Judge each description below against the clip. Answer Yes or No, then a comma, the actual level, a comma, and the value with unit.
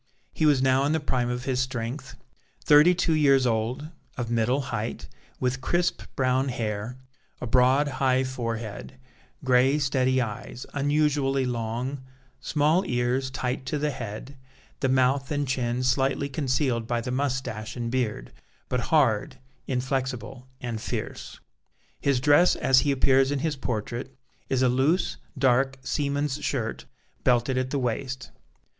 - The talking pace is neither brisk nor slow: Yes, average, 145 wpm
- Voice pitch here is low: Yes, low, 130 Hz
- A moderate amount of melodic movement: No, narrow, 2.1 semitones